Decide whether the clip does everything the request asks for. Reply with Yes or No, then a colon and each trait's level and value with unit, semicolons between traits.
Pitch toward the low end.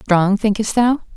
No: high, 210 Hz